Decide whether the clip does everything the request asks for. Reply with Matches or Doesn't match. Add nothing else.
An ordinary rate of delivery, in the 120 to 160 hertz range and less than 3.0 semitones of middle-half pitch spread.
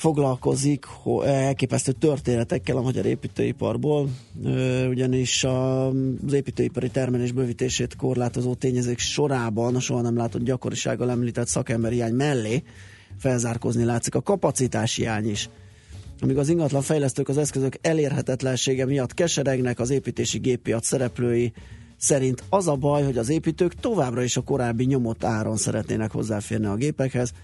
Matches